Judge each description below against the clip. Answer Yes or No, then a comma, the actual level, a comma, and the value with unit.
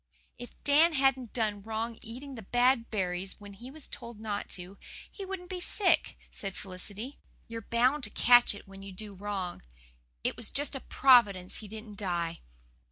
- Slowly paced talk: No, average, 175 wpm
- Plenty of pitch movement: No, average, 4.8 semitones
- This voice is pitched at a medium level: No, high, 225 Hz